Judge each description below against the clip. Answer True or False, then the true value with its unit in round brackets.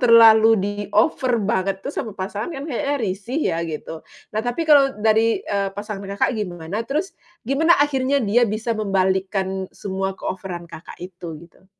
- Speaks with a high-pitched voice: True (210 Hz)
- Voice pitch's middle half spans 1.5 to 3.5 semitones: False (4.2 semitones)